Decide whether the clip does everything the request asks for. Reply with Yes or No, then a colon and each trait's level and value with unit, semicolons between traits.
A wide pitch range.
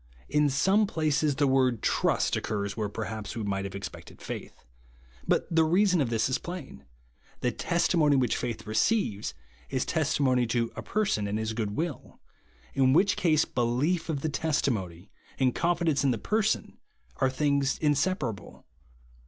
Yes: wide, 6.3 semitones